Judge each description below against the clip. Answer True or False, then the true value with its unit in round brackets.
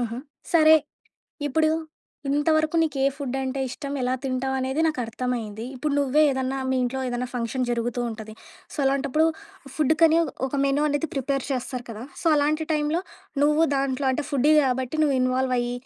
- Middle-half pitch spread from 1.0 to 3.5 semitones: True (3.0 semitones)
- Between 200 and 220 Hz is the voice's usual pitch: False (270 Hz)